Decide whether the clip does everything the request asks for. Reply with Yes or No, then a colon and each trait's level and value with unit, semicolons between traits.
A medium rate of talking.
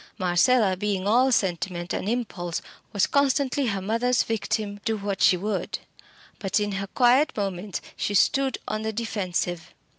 Yes: average, 150 wpm